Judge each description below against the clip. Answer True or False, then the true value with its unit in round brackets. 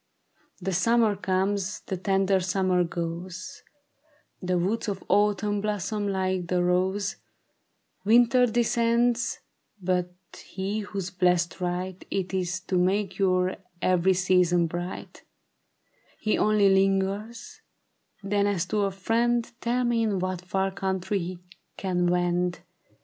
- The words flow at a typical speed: False (120 wpm)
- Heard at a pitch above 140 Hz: True (190 Hz)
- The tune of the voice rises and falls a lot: False (2.4 semitones)